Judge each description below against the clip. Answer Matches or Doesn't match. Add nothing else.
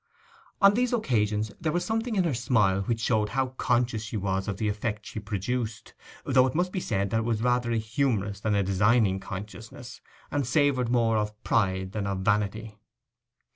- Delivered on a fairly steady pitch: Doesn't match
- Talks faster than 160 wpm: Matches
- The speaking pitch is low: Matches